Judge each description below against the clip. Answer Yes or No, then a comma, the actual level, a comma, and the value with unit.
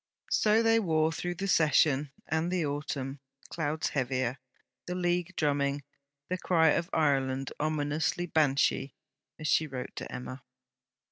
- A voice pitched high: No, medium, 155 Hz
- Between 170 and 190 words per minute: No, slow, 135 wpm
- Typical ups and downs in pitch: Yes, average, 3.8 semitones